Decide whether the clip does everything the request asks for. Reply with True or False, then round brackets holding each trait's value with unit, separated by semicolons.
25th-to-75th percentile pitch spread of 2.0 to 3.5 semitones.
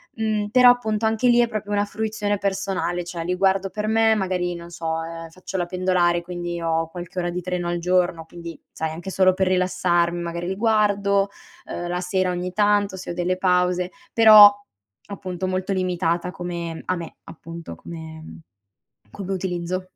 True (2.5 semitones)